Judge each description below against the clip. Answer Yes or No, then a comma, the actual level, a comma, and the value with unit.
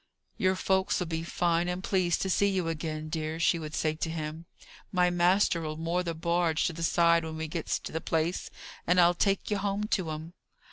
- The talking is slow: No, fast, 205 wpm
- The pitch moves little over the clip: Yes, narrow, 2.0 semitones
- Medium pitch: Yes, medium, 170 Hz